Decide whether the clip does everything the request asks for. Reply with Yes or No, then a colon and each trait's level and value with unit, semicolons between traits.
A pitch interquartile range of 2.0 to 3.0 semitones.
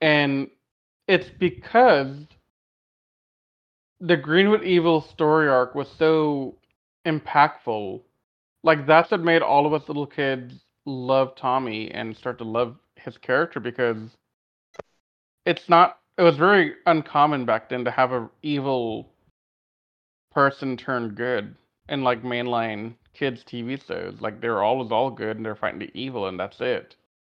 No: average, 4.4 semitones